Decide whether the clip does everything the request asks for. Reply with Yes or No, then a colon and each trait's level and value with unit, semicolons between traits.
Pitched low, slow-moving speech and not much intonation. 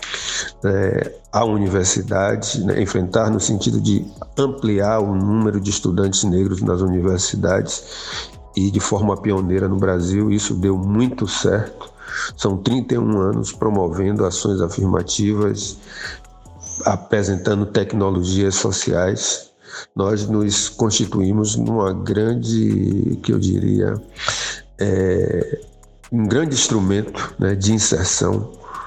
Yes: low, 100 Hz; slow, 105 wpm; narrow, 2.1 semitones